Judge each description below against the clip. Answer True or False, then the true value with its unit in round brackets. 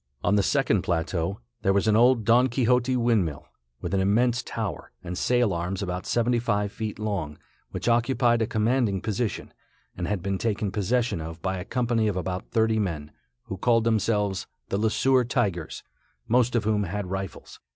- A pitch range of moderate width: True (3.8 semitones)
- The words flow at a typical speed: True (180 wpm)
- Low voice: True (105 Hz)